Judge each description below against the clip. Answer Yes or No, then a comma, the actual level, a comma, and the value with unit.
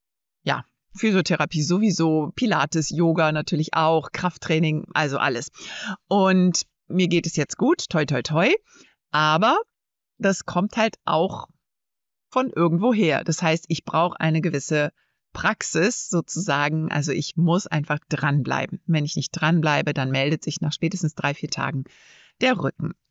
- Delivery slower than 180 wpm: Yes, average, 140 wpm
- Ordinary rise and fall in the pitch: Yes, average, 3.2 semitones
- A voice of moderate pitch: Yes, medium, 165 Hz